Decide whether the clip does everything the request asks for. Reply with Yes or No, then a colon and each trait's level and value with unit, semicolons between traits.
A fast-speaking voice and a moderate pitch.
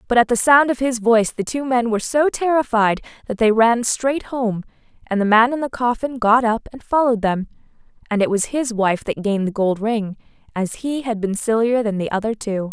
No: fast, 225 wpm; high, 230 Hz